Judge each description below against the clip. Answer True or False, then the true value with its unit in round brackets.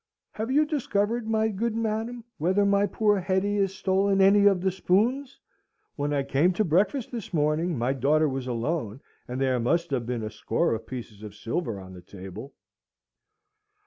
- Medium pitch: True (180 Hz)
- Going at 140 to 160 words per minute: False (175 wpm)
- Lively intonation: True (8.3 semitones)